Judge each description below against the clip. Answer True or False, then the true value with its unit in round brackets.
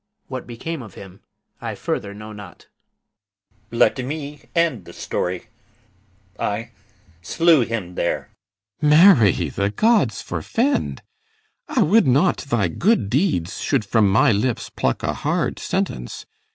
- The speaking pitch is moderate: False (120 Hz)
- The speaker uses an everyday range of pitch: False (7.8 semitones)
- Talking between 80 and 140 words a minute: True (135 wpm)